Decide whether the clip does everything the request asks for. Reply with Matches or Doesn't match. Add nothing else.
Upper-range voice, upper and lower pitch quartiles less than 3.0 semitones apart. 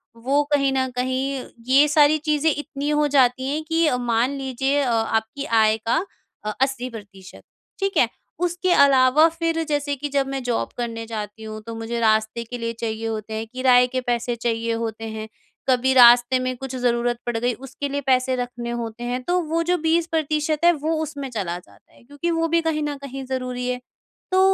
Doesn't match